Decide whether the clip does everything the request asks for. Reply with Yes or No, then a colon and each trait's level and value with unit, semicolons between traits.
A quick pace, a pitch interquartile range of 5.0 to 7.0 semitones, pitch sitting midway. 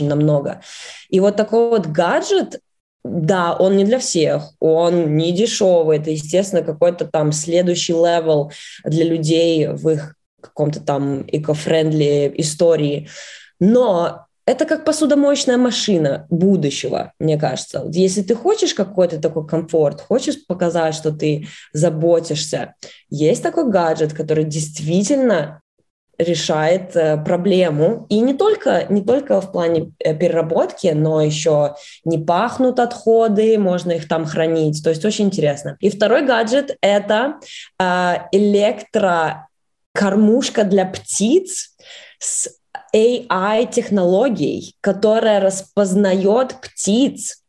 No: average, 115 wpm; wide, 5.6 semitones; medium, 180 Hz